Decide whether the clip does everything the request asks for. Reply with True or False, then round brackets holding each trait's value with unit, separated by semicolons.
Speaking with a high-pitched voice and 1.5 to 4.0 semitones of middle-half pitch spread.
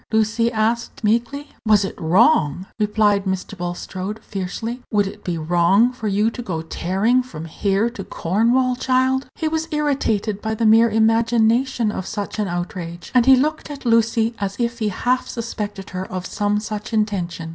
True (215 Hz; 3.5 semitones)